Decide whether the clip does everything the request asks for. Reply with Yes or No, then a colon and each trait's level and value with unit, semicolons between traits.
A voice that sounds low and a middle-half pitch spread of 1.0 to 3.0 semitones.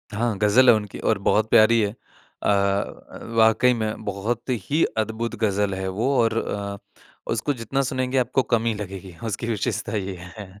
Yes: low, 110 Hz; average, 2.7 semitones